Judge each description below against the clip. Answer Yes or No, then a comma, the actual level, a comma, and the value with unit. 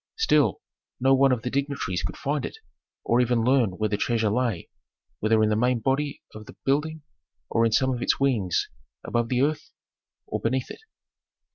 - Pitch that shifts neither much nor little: Yes, average, 3.7 semitones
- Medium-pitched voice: No, low, 125 Hz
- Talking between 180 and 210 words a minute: Yes, average, 185 wpm